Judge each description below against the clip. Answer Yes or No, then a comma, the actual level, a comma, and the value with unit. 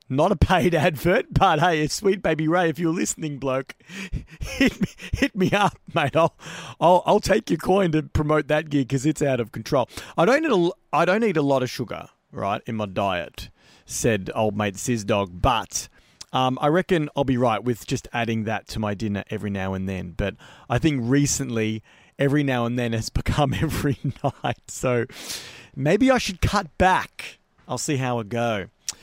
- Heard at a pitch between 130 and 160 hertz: Yes, medium, 140 Hz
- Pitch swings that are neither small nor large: No, wide, 6.0 semitones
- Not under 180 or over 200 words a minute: Yes, average, 190 wpm